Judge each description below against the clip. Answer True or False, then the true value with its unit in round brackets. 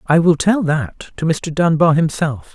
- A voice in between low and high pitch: True (160 Hz)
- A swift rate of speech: False (190 wpm)